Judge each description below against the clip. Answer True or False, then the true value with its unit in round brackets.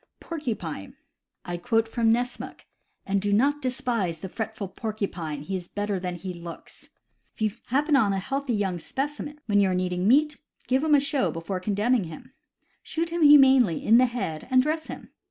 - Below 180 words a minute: False (190 wpm)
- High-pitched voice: True (220 Hz)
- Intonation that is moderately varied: False (6.5 semitones)